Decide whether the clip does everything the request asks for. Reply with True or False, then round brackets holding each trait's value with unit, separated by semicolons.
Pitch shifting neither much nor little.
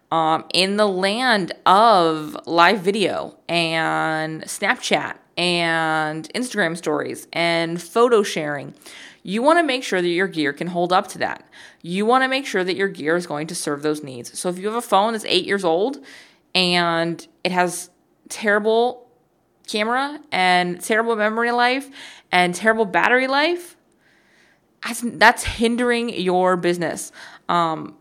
False (5.8 semitones)